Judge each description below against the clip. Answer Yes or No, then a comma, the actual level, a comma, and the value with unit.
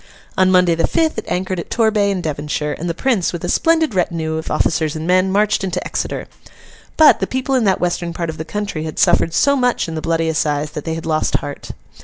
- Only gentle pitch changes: No, average, 4.4 semitones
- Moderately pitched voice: Yes, medium, 175 Hz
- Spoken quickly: Yes, fast, 235 wpm